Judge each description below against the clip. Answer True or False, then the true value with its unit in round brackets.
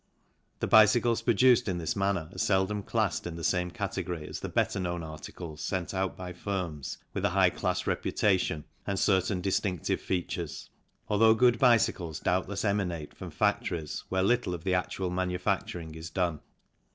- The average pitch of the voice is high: False (95 Hz)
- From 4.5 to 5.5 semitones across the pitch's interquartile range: False (2.8 semitones)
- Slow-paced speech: False (165 wpm)